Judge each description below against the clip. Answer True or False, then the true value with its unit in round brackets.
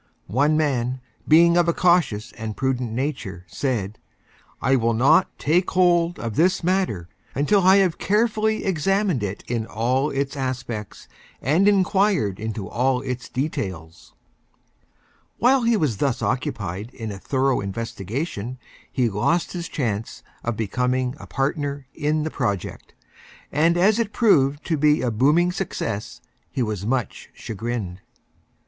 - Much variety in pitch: True (7.1 semitones)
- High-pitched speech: False (135 Hz)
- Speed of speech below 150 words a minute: True (140 wpm)